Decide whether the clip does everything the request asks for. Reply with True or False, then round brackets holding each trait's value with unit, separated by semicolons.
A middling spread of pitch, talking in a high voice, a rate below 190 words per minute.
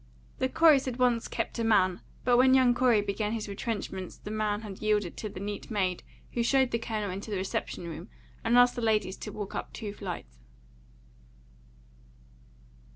True (3.4 semitones; 215 Hz; 180 wpm)